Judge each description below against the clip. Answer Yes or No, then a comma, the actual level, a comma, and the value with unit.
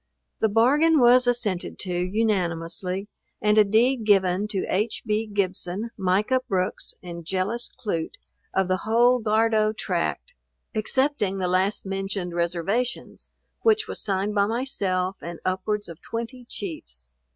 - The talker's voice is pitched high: Yes, high, 205 Hz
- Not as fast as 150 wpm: Yes, slow, 135 wpm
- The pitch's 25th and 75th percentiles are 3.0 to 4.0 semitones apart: Yes, average, 3.7 semitones